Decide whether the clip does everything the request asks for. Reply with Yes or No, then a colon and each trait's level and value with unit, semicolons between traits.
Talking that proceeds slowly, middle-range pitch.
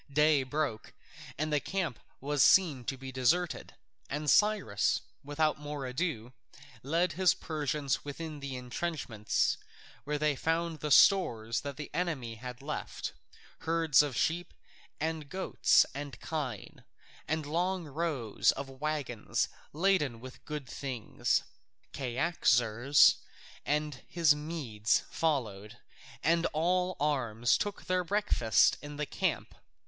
Yes: slow, 120 wpm; medium, 150 Hz